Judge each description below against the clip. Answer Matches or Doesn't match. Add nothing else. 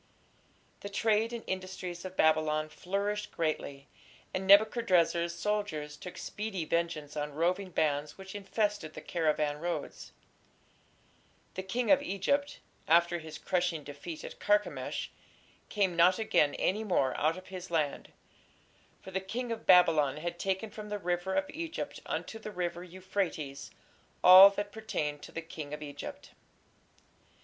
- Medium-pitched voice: Matches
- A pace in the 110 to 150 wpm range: Matches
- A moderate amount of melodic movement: Matches